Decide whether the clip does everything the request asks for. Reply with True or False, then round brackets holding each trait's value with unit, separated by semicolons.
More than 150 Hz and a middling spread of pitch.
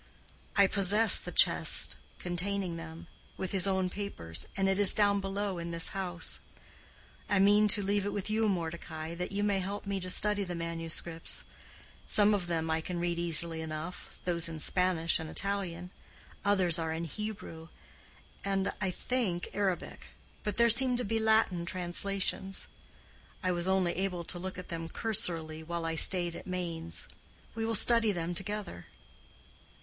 True (185 Hz; 3.1 semitones)